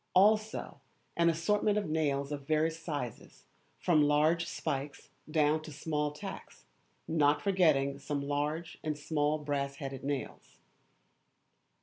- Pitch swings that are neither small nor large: No, narrow, 2.3 semitones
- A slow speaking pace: Yes, slow, 120 wpm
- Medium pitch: Yes, medium, 150 Hz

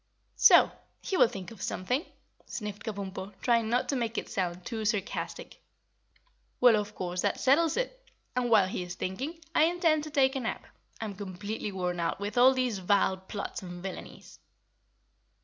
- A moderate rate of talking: Yes, average, 170 wpm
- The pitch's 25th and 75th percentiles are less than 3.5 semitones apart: No, average, 5.1 semitones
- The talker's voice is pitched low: No, high, 210 Hz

